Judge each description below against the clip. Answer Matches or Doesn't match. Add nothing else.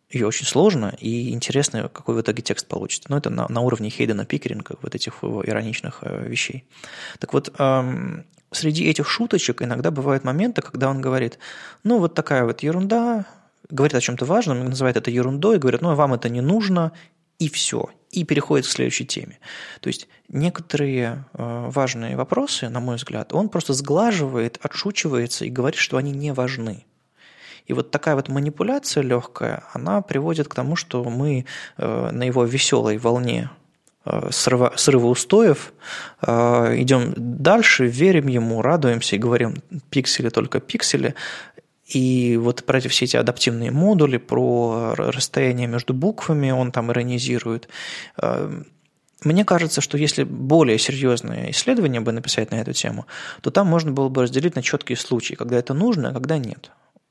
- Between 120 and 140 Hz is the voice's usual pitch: Matches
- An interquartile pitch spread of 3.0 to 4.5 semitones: Doesn't match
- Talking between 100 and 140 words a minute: Doesn't match